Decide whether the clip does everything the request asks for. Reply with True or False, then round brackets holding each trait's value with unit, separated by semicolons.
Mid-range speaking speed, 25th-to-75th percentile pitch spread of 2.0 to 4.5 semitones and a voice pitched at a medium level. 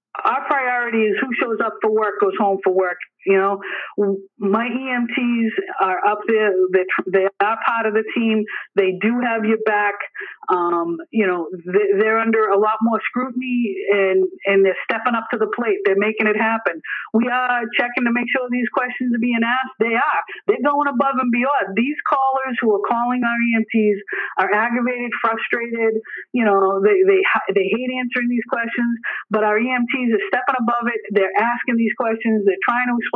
False (190 wpm; 3.2 semitones; 225 Hz)